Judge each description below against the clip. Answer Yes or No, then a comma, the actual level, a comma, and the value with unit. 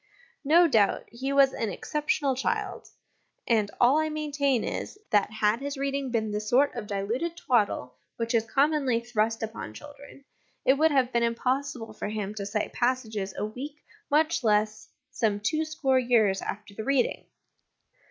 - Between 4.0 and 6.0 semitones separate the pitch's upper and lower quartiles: Yes, average, 4.6 semitones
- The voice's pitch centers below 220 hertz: No, high, 245 Hz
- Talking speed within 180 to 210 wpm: No, average, 160 wpm